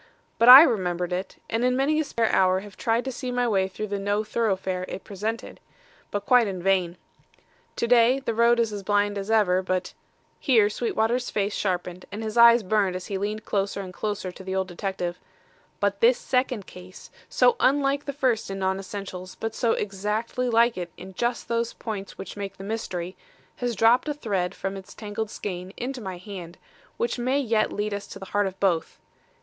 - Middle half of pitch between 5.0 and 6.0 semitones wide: No, average, 3.7 semitones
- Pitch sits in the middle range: No, high, 205 Hz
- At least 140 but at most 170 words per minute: No, fast, 205 wpm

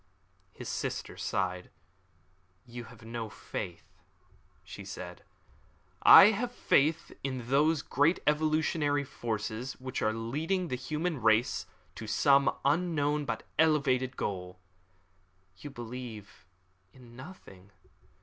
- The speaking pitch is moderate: No, low, 130 Hz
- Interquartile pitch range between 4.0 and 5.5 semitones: Yes, average, 5.1 semitones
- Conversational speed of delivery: No, slow, 110 wpm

